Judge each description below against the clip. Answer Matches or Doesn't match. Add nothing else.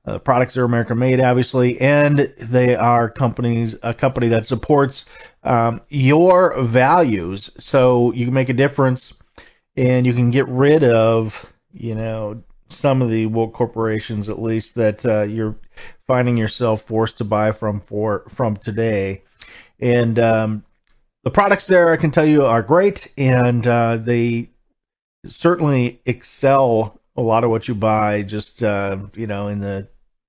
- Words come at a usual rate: Matches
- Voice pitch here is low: Matches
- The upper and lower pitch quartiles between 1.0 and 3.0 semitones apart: Matches